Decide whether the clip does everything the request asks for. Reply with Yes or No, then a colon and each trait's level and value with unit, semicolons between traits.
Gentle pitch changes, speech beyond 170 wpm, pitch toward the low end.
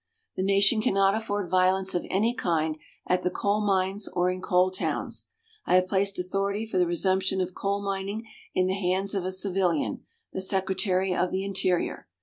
No: narrow, 1.4 semitones; average, 180 wpm; high, 190 Hz